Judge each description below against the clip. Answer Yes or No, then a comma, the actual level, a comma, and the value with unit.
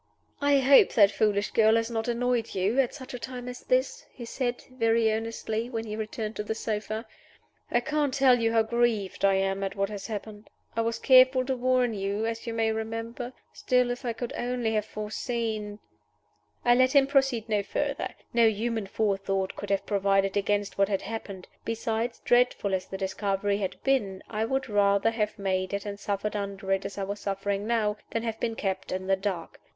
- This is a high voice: Yes, high, 220 Hz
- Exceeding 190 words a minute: Yes, average, 200 wpm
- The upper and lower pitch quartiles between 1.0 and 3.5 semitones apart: Yes, average, 3.1 semitones